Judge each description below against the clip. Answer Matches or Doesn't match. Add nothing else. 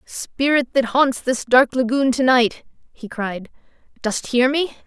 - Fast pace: Doesn't match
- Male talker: Doesn't match